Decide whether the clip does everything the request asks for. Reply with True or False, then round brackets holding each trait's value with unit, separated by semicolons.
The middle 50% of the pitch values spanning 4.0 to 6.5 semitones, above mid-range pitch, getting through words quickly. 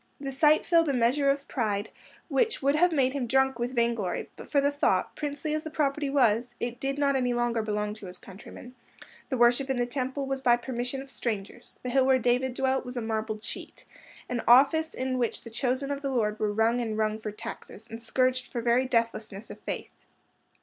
False (3.0 semitones; 250 Hz; 210 wpm)